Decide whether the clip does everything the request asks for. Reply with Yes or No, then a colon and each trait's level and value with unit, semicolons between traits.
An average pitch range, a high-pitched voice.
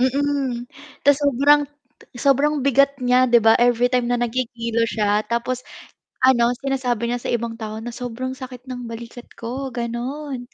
No: narrow, 2.2 semitones; high, 245 Hz